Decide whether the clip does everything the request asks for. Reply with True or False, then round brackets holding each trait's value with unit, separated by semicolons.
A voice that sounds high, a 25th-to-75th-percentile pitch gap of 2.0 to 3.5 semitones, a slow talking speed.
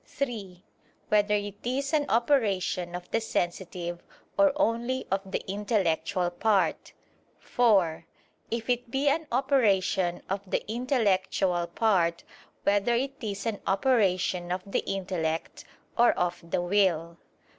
False (200 Hz; 4.9 semitones; 125 wpm)